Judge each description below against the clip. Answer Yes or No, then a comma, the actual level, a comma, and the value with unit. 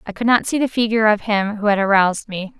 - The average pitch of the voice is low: No, high, 210 Hz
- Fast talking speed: Yes, fast, 280 wpm